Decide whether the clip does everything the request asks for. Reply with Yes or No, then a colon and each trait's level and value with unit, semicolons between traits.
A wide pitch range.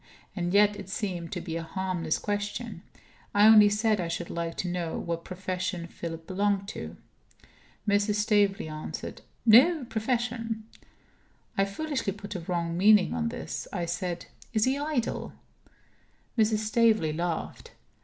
No: average, 3.9 semitones